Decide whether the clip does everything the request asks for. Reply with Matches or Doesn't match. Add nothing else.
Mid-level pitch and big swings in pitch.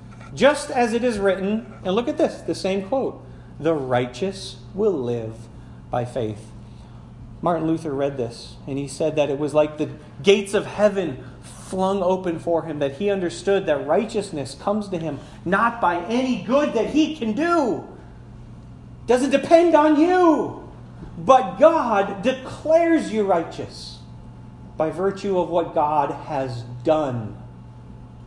Matches